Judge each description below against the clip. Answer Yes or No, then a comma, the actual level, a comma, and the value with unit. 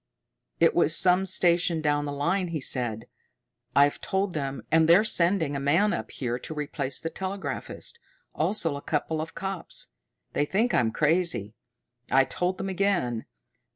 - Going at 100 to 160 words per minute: Yes, average, 155 wpm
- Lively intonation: No, average, 4.8 semitones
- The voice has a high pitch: No, medium, 160 Hz